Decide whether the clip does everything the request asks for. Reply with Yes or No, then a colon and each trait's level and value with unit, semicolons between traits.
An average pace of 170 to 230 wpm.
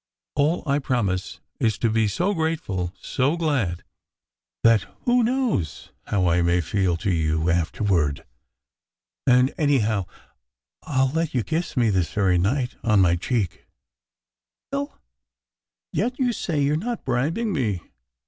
No: average, 150 wpm